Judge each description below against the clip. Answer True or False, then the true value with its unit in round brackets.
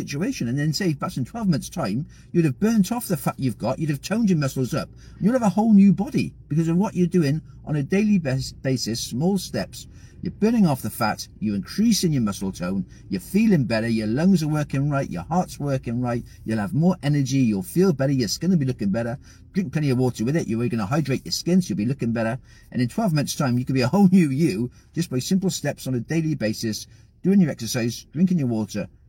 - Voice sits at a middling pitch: True (145 Hz)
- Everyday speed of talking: False (245 wpm)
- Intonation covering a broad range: True (7.2 semitones)